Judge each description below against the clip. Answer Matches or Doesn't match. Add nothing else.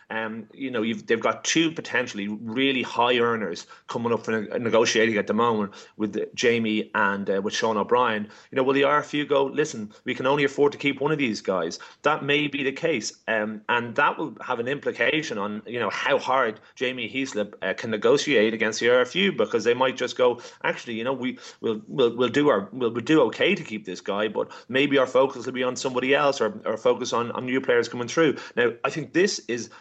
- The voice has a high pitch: Doesn't match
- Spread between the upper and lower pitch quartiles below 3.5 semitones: Doesn't match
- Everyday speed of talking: Doesn't match